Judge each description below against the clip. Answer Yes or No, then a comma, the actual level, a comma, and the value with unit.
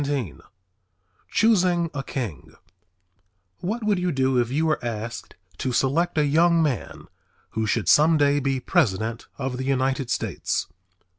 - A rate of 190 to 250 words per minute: No, average, 145 wpm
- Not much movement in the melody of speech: No, average, 4.9 semitones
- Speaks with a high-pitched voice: No, medium, 140 Hz